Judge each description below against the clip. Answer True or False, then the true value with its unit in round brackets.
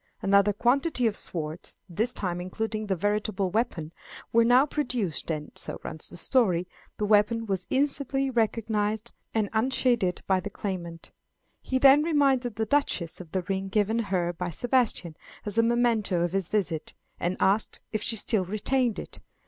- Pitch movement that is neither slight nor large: True (4.6 semitones)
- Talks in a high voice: True (210 Hz)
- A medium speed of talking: True (165 wpm)